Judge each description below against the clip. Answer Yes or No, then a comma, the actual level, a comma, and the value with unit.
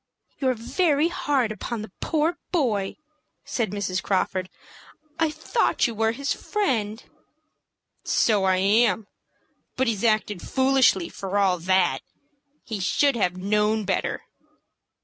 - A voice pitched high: Yes, high, 220 Hz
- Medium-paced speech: No, slow, 125 wpm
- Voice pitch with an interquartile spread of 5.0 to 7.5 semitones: Yes, wide, 5.4 semitones